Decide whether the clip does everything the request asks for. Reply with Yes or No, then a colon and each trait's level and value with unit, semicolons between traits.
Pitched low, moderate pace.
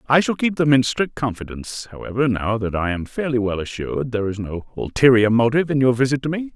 No: low, 125 Hz; fast, 230 wpm